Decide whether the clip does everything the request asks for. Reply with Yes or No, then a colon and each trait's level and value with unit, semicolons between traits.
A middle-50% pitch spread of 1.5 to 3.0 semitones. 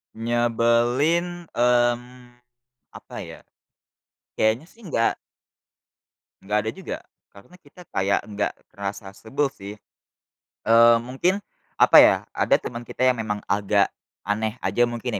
Yes: average, 2.7 semitones